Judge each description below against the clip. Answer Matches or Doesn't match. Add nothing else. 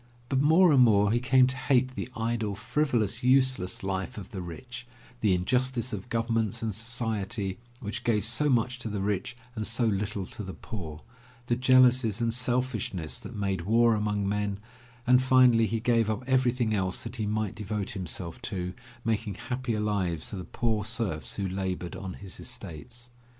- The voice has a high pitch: Doesn't match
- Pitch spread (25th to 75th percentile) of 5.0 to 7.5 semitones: Doesn't match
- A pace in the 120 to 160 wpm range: Doesn't match